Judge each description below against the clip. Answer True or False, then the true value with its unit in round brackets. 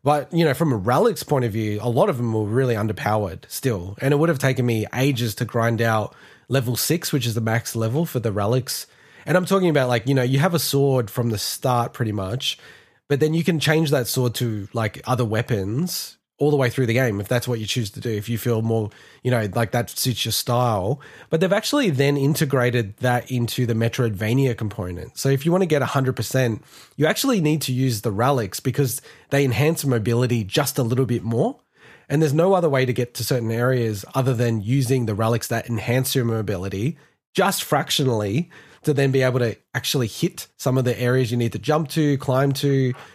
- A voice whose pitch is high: False (125 Hz)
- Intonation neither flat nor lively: True (3.6 semitones)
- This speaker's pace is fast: True (220 wpm)